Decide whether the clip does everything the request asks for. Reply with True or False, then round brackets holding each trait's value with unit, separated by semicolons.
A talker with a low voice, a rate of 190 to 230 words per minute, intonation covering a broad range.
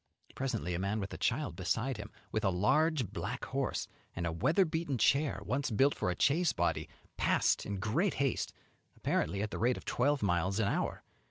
True (115 Hz; 195 wpm; 6.4 semitones)